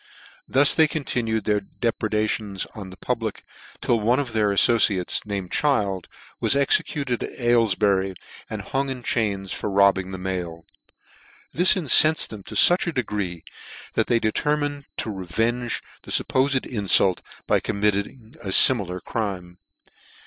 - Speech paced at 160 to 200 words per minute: No, average, 140 wpm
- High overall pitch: No, low, 110 Hz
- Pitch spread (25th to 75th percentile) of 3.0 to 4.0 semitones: No, average, 4.6 semitones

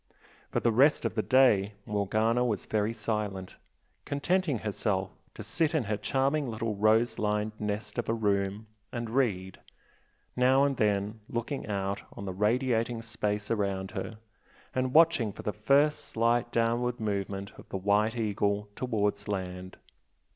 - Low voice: Yes, low, 110 Hz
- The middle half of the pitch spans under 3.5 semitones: Yes, average, 3.0 semitones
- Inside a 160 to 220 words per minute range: No, average, 150 wpm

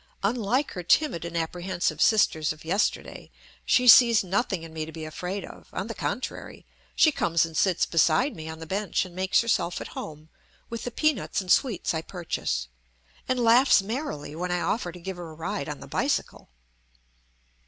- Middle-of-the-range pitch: Yes, medium, 180 Hz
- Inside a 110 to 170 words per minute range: No, average, 185 wpm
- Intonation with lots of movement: Yes, wide, 5.8 semitones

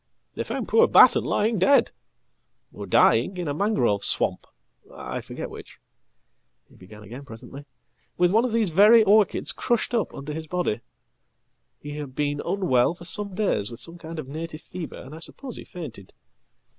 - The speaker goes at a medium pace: Yes, average, 160 wpm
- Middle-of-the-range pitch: Yes, medium, 165 Hz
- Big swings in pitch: Yes, wide, 6.6 semitones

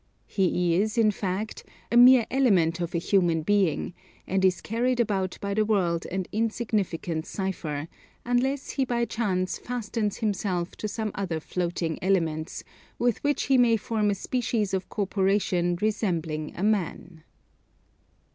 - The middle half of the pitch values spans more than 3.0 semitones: Yes, average, 4.2 semitones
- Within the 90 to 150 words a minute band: Yes, average, 140 wpm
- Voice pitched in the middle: No, high, 200 Hz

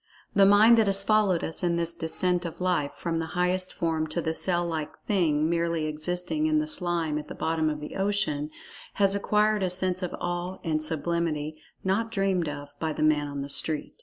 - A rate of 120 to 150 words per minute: No, fast, 205 wpm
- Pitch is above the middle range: No, medium, 170 Hz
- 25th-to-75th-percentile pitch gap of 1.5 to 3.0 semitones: No, average, 3.5 semitones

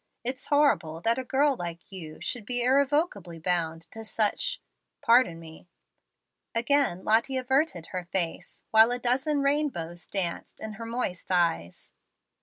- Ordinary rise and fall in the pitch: No, wide, 7.3 semitones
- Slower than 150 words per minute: Yes, average, 140 wpm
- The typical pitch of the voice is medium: No, high, 225 Hz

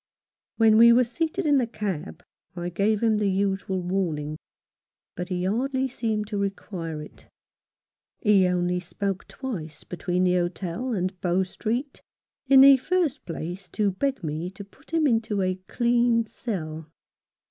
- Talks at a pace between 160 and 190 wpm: No, average, 150 wpm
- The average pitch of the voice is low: No, high, 200 Hz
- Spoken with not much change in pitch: No, average, 4.8 semitones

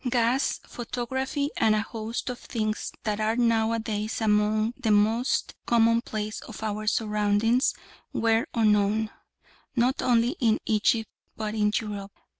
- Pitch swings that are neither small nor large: No, narrow, 1.7 semitones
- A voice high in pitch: Yes, high, 220 Hz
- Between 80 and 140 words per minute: Yes, slow, 135 wpm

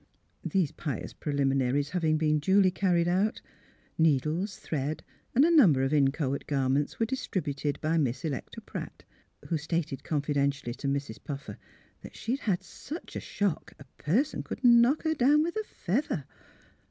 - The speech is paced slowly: No, average, 165 wpm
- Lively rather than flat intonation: Yes, wide, 6.3 semitones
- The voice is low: No, medium, 155 Hz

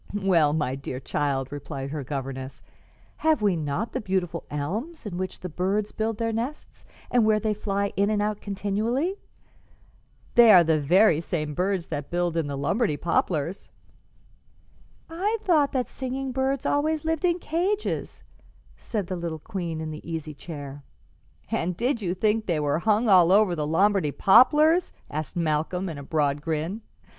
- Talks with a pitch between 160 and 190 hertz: Yes, medium, 185 Hz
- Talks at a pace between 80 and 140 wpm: No, average, 165 wpm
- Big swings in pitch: Yes, wide, 6.5 semitones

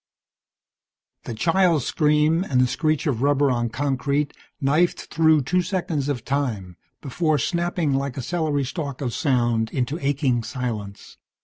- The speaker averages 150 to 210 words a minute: No, average, 140 wpm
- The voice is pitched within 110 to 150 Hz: Yes, medium, 140 Hz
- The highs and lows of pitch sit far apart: No, average, 4.0 semitones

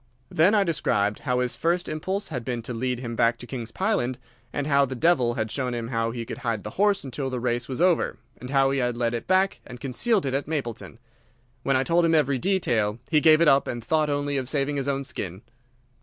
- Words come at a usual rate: No, fast, 240 wpm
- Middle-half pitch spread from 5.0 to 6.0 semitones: No, average, 4.4 semitones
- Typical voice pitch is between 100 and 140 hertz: Yes, low, 135 Hz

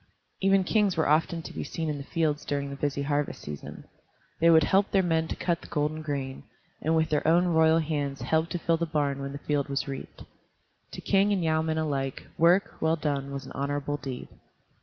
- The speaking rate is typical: No, fast, 215 wpm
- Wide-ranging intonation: No, average, 2.7 semitones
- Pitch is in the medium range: Yes, medium, 155 Hz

